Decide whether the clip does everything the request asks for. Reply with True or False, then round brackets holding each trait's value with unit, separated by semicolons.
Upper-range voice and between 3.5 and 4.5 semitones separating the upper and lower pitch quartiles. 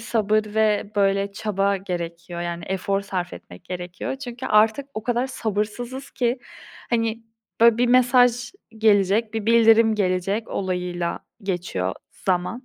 True (210 Hz; 3.9 semitones)